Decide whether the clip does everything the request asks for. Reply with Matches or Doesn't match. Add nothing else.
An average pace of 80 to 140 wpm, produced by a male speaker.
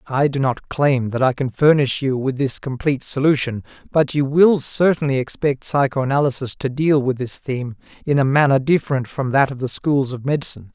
Doesn't match